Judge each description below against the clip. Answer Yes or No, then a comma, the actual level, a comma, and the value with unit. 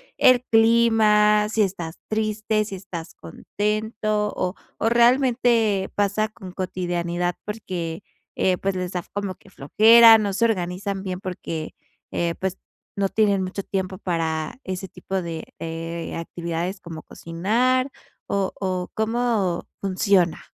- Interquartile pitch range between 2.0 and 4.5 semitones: Yes, average, 3.3 semitones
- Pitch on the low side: No, high, 195 Hz